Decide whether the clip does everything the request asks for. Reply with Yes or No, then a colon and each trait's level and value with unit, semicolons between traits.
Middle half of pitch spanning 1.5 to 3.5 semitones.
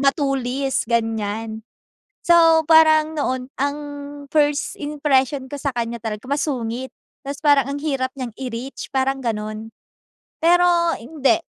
No: average, 3.9 semitones